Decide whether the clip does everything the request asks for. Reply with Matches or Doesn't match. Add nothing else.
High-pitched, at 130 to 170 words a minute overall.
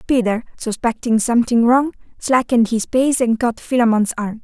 Matches